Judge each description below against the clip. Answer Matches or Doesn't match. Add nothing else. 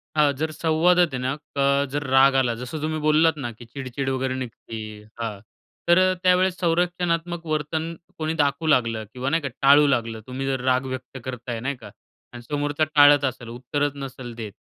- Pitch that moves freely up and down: Doesn't match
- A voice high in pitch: Doesn't match